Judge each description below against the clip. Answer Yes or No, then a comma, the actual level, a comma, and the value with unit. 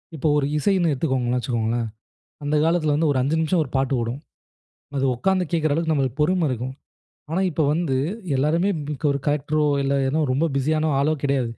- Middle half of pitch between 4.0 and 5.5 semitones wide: No, average, 3.3 semitones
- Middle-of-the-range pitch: Yes, medium, 145 Hz